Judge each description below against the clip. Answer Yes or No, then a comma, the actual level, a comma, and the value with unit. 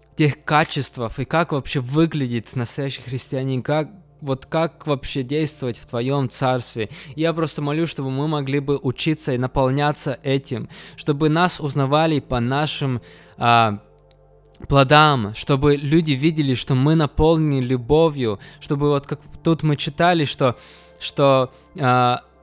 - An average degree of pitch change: Yes, average, 3.1 semitones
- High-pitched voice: No, medium, 140 Hz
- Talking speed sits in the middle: Yes, average, 135 wpm